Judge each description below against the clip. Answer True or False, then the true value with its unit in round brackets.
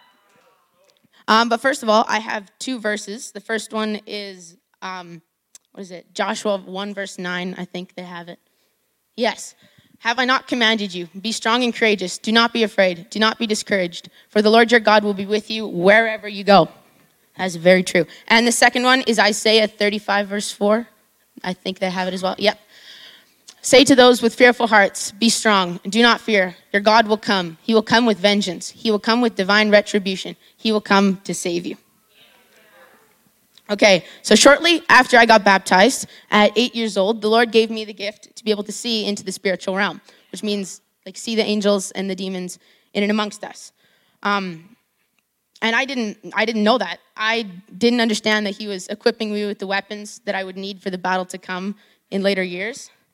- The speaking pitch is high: True (210 Hz)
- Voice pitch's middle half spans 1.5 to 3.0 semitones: True (2.6 semitones)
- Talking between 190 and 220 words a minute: True (200 wpm)